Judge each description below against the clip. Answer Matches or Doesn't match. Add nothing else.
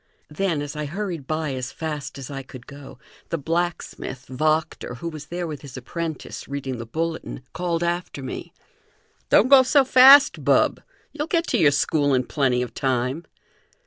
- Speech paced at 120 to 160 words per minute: Doesn't match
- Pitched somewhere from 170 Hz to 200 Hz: Doesn't match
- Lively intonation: Doesn't match